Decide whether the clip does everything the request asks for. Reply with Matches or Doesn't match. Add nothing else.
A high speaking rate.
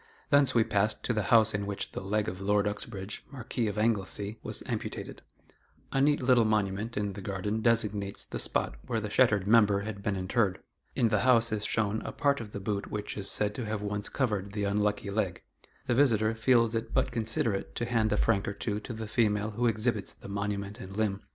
Matches